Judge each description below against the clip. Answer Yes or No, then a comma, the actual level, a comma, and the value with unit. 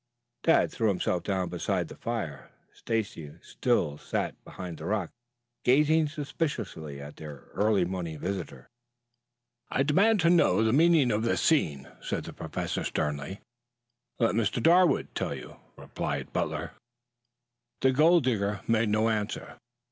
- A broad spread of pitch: Yes, wide, 8.4 semitones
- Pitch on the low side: Yes, low, 110 Hz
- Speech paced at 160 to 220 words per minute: No, average, 140 wpm